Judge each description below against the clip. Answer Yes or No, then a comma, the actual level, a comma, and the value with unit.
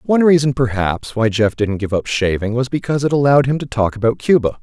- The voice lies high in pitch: No, low, 125 Hz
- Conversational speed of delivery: No, fast, 235 wpm